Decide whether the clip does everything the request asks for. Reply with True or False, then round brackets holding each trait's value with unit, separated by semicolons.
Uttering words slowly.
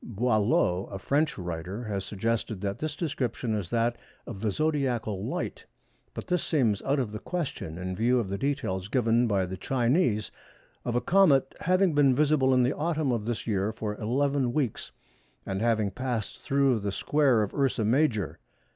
False (175 wpm)